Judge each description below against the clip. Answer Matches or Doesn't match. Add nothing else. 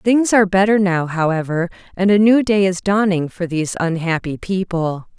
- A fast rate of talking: Doesn't match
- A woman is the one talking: Matches